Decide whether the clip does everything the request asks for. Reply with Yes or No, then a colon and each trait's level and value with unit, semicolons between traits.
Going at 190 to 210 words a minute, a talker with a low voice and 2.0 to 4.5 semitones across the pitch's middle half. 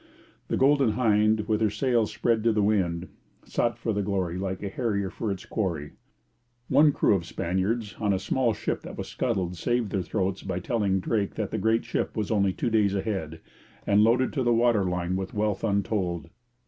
Yes: average, 200 wpm; low, 105 Hz; average, 3.1 semitones